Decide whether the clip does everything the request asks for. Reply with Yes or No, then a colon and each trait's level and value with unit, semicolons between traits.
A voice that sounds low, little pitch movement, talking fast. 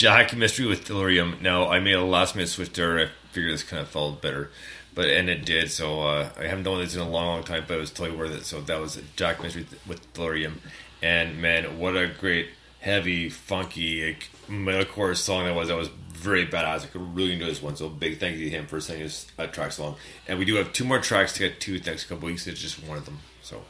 Yes: very low, 85 Hz; narrow, 2.3 semitones; fast, 265 wpm